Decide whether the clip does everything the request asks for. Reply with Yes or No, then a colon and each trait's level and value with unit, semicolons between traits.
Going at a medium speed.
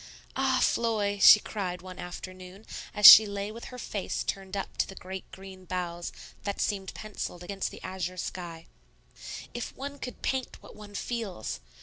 Yes: average, 165 wpm